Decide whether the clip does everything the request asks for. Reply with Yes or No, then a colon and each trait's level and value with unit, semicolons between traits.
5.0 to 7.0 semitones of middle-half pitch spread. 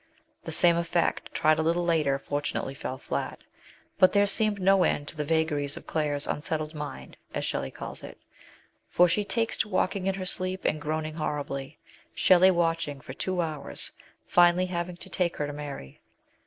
No: average, 3.7 semitones